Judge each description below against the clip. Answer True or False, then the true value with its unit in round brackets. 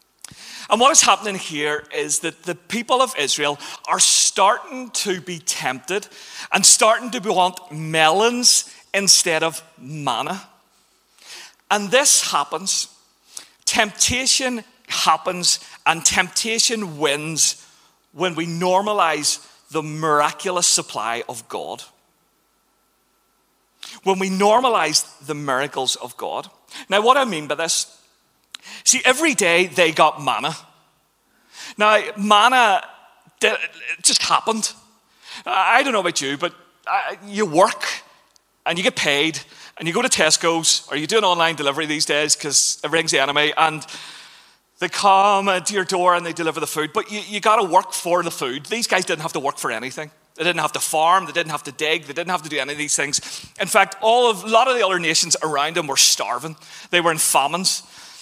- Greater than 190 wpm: False (165 wpm)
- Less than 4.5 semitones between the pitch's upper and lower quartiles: False (5.2 semitones)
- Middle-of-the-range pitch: True (175 Hz)